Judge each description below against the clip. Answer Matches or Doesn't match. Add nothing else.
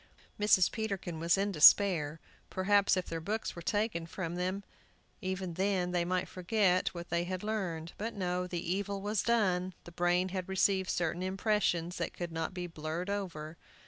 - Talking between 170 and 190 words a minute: Matches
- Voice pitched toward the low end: Doesn't match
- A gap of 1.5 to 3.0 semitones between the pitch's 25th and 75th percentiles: Matches